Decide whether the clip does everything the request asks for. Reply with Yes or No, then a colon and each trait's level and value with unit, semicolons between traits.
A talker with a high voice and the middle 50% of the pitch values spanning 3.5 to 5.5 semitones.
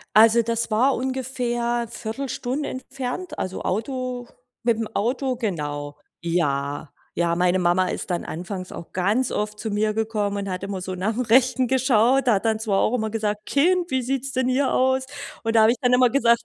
Yes: high, 225 Hz; average, 4.4 semitones